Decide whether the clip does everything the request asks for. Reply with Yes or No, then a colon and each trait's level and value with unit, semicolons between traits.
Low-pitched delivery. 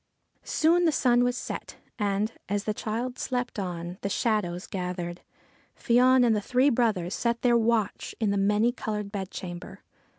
No: high, 215 Hz